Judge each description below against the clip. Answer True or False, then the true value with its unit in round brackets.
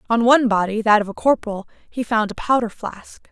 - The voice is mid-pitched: False (225 Hz)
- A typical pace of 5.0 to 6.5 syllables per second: True (5.7 syllables/s)